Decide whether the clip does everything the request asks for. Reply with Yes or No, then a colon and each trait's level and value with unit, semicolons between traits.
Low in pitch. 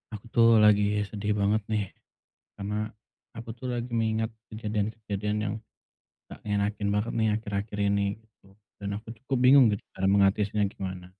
Yes: low, 105 Hz